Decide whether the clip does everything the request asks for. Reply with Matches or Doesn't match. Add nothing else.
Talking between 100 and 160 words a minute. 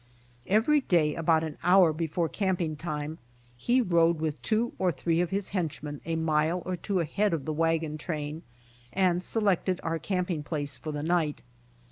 Doesn't match